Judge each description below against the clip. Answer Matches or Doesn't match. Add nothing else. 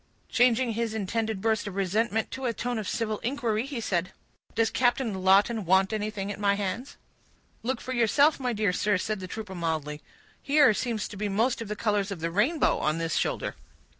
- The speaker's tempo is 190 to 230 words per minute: Matches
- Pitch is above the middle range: Matches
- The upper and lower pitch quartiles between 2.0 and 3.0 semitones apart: Doesn't match